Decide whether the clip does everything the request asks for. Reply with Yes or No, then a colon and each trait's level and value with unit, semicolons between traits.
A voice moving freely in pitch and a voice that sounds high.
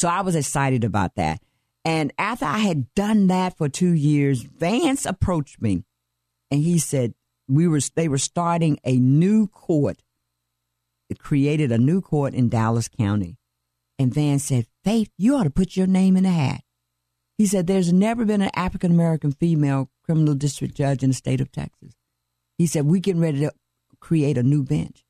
No: wide, 6.4 semitones; medium, 145 Hz